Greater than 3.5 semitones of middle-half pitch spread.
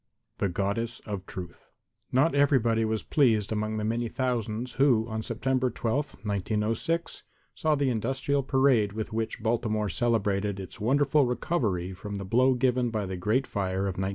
Yes: average, 3.9 semitones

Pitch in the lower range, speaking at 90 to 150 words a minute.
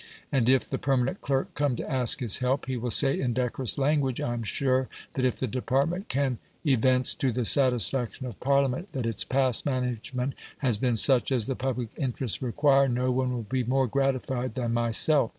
No: low, 130 Hz; average, 195 wpm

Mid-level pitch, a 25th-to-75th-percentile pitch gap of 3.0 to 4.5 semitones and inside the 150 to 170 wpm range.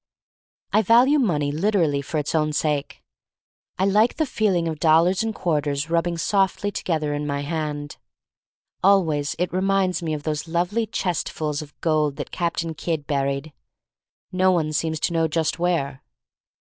Yes: medium, 165 Hz; average, 3.8 semitones; average, 155 wpm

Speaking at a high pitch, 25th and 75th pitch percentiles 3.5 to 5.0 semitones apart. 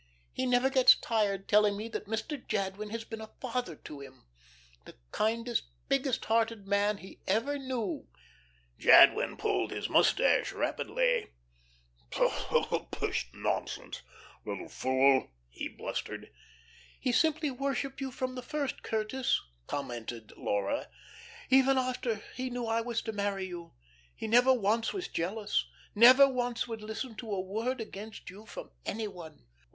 Yes: high, 225 Hz; average, 4.3 semitones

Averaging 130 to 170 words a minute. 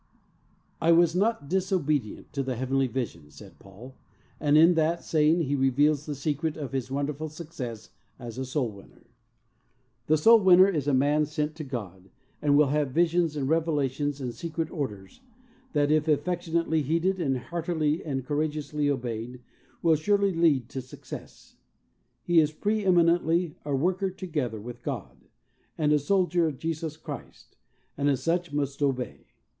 Yes: average, 160 wpm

